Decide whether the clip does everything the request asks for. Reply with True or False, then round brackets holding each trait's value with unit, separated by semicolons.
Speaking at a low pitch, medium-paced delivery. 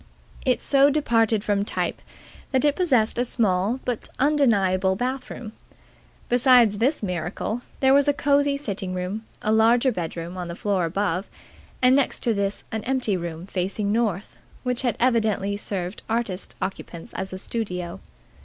False (215 Hz; 155 wpm)